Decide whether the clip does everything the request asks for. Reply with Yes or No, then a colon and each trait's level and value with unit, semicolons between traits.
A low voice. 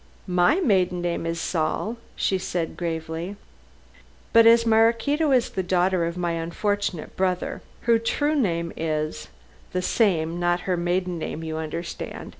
No: medium, 180 Hz